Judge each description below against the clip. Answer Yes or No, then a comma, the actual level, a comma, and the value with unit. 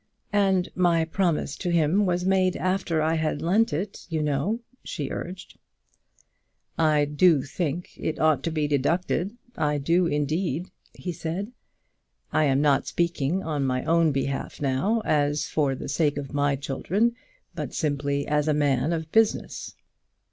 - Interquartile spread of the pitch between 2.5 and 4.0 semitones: Yes, average, 3.7 semitones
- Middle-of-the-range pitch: Yes, medium, 160 Hz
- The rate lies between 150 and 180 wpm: Yes, average, 155 wpm